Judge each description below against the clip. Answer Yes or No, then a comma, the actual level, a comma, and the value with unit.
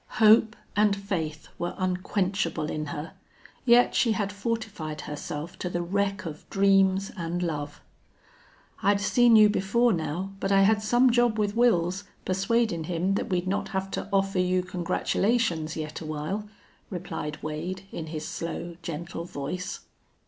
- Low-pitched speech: No, medium, 185 Hz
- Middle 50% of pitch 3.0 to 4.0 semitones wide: Yes, average, 3.6 semitones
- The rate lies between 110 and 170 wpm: Yes, average, 150 wpm